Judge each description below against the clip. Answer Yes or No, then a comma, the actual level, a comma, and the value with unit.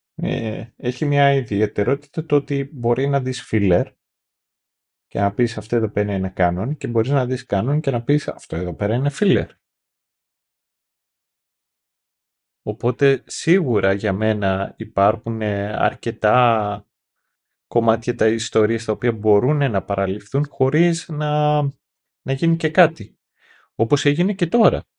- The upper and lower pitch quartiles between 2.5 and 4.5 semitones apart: No, average, 5.1 semitones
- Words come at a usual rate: Yes, average, 130 wpm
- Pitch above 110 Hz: Yes, low, 120 Hz